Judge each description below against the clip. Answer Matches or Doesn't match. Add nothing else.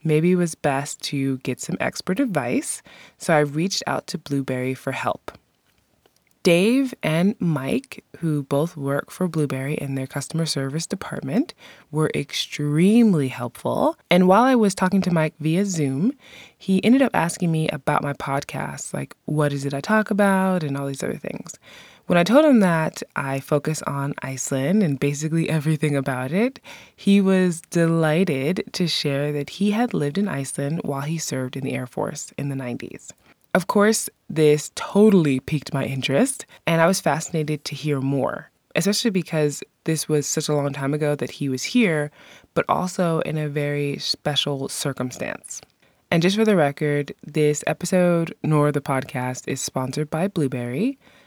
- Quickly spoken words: Doesn't match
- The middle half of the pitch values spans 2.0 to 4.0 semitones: Doesn't match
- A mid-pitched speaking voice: Matches